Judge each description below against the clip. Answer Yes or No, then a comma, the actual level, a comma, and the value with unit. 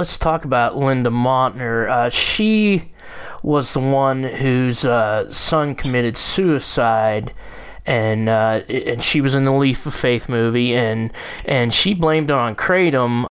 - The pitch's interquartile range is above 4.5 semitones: No, average, 3.8 semitones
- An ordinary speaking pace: Yes, average, 150 wpm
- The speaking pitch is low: Yes, low, 130 Hz